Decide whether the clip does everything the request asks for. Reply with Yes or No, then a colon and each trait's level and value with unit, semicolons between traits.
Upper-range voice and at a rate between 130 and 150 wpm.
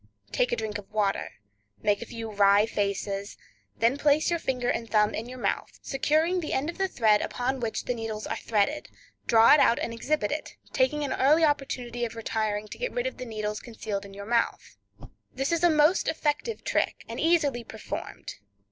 No: high, 240 Hz; average, 200 wpm